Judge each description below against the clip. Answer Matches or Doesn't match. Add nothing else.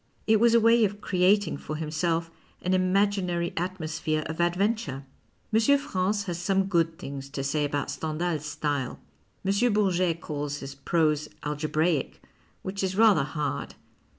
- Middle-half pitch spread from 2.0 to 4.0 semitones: Doesn't match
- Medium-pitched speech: Matches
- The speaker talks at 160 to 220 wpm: Doesn't match